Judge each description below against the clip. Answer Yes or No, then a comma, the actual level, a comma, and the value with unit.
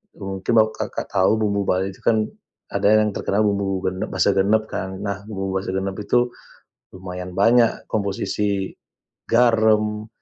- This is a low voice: Yes, low, 100 Hz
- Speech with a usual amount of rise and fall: No, narrow, 2.2 semitones